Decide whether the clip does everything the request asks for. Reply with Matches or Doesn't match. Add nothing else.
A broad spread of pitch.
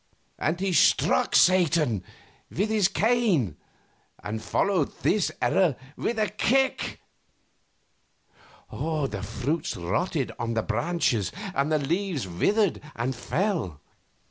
Matches